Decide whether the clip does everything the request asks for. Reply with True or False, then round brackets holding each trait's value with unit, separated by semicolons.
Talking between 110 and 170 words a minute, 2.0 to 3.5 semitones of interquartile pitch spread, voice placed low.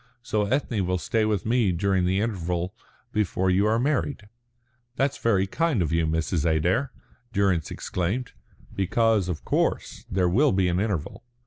False (155 wpm; 4.1 semitones; 95 Hz)